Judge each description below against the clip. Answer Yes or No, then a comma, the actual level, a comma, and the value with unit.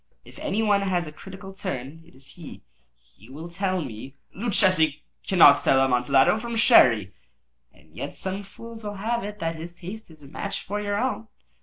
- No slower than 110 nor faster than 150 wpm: No, average, 185 wpm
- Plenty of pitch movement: Yes, wide, 6.1 semitones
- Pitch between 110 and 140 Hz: No, medium, 185 Hz